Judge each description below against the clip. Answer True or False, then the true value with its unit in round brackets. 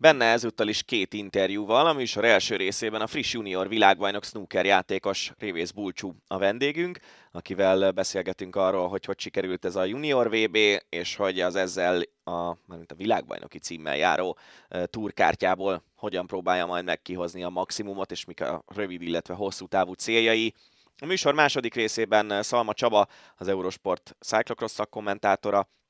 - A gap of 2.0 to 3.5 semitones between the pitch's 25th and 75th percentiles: True (2.9 semitones)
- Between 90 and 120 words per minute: False (150 wpm)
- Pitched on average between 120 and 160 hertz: False (100 Hz)